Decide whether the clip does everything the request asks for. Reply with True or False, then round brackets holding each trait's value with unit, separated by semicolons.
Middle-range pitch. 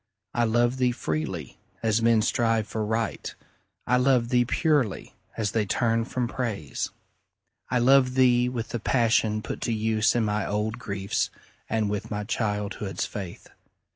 False (115 Hz)